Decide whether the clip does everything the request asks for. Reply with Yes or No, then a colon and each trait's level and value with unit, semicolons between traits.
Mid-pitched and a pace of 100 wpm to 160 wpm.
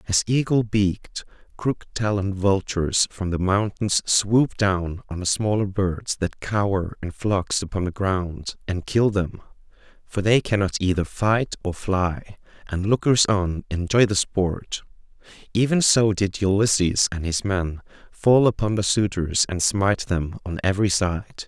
No: low, 100 Hz; average, 150 wpm